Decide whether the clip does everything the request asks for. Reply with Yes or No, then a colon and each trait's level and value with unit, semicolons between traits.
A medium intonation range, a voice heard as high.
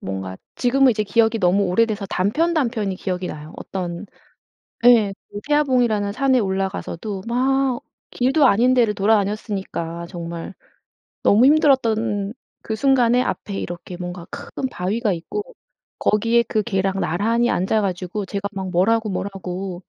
Yes: average, 4.2 semitones; high, 205 Hz